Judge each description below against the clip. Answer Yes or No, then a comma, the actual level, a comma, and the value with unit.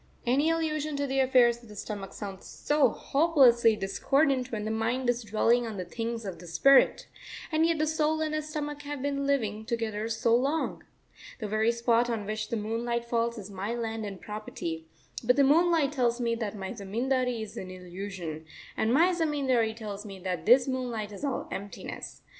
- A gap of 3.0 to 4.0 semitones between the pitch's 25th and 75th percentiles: No, average, 4.6 semitones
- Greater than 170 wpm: Yes, average, 190 wpm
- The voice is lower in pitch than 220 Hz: No, high, 235 Hz